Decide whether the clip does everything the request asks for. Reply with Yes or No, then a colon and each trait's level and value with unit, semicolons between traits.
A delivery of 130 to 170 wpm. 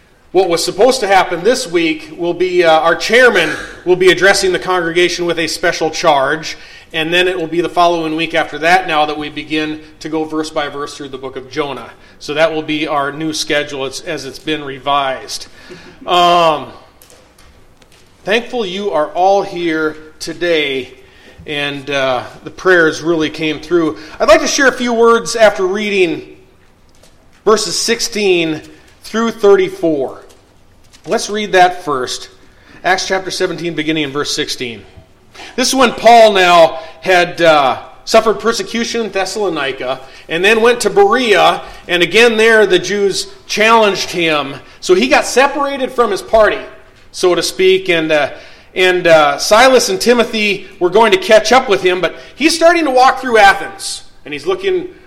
Yes: average, 165 wpm